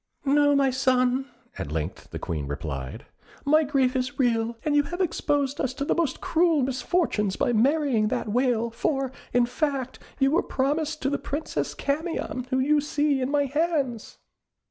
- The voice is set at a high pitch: Yes, very high, 270 Hz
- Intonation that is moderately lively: Yes, average, 3.1 semitones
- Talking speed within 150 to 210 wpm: Yes, average, 170 wpm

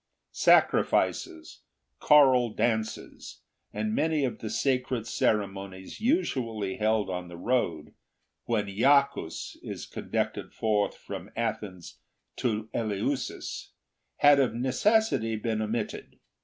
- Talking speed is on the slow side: Yes, slow, 100 wpm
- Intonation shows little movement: No, average, 4.0 semitones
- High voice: No, low, 110 Hz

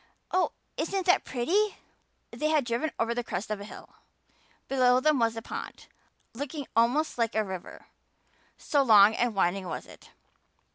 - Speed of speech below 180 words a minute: Yes, average, 160 wpm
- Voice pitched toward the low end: No, high, 245 Hz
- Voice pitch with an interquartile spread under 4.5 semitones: No, wide, 5.5 semitones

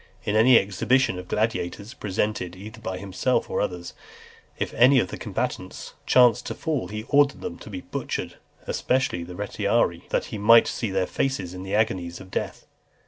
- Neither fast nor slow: Yes, average, 180 wpm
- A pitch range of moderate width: Yes, average, 4.2 semitones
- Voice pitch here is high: No, low, 105 Hz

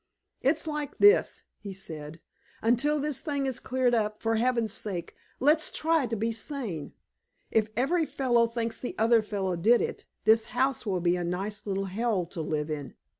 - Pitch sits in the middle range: No, high, 225 Hz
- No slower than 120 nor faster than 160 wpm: No, average, 175 wpm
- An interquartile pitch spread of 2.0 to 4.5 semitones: No, average, 5.2 semitones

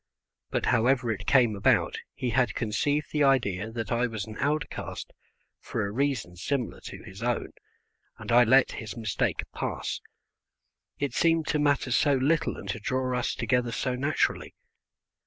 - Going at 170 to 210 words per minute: No, average, 160 wpm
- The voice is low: Yes, low, 125 Hz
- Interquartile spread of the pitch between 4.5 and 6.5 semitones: No, average, 3.7 semitones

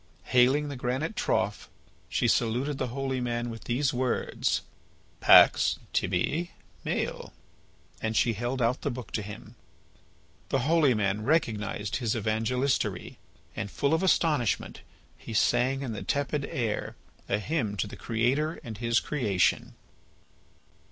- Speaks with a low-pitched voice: Yes, low, 120 Hz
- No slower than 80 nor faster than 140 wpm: Yes, slow, 135 wpm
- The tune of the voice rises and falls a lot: No, average, 3.9 semitones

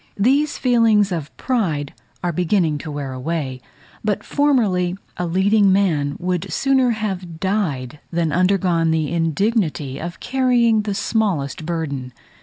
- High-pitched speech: No, medium, 180 Hz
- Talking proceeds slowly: Yes, slow, 130 wpm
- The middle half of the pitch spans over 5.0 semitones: Yes, wide, 5.4 semitones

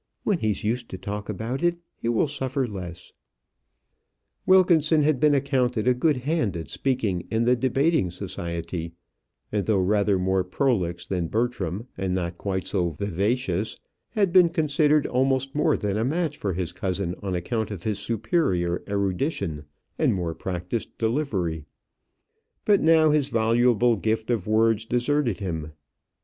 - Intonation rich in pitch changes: Yes, wide, 6.4 semitones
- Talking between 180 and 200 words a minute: No, average, 150 wpm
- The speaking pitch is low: Yes, low, 110 Hz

